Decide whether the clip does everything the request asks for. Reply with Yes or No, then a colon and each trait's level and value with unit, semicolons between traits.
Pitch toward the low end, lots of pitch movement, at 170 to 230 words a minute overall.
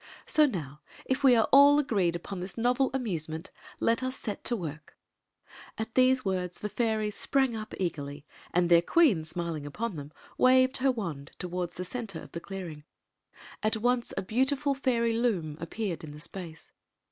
No: high, 210 Hz; wide, 6.8 semitones; average, 175 wpm